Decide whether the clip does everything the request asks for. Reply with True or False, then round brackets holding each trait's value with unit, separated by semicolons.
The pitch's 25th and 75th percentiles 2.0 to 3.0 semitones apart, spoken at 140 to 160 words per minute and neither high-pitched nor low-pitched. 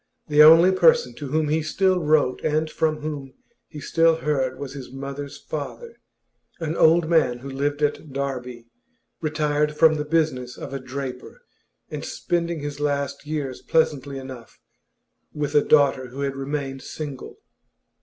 True (2.5 semitones; 155 wpm; 145 Hz)